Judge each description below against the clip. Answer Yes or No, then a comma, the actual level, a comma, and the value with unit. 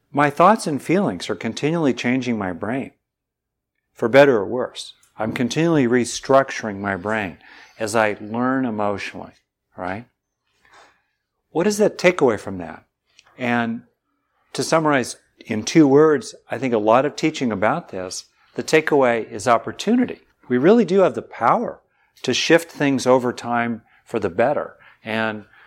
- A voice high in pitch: No, low, 125 Hz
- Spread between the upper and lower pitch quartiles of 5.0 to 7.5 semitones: Yes, wide, 5.4 semitones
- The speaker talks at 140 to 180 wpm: Yes, average, 145 wpm